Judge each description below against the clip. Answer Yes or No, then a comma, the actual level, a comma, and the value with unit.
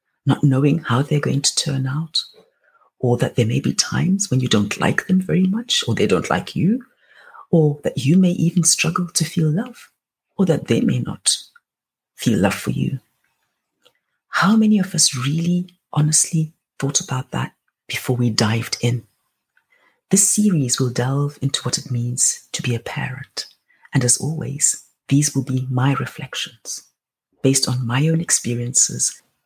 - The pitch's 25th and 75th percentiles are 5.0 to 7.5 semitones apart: Yes, average, 5.3 semitones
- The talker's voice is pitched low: No, medium, 145 Hz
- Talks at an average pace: Yes, average, 165 wpm